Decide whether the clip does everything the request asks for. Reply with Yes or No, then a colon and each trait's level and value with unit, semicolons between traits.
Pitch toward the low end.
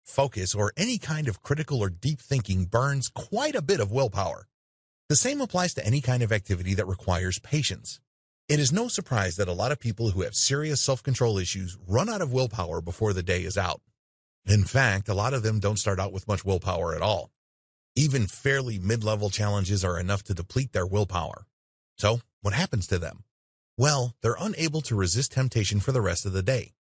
Yes: low, 105 Hz